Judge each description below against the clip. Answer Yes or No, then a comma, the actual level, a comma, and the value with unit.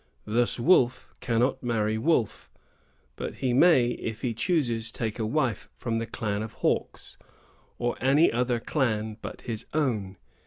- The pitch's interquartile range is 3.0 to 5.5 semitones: No, narrow, 2.6 semitones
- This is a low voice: Yes, low, 120 Hz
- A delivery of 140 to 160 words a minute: Yes, average, 150 wpm